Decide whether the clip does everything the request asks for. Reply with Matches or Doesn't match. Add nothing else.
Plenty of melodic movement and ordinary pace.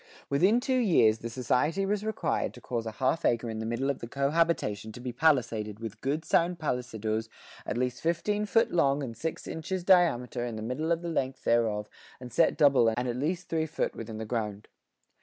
Doesn't match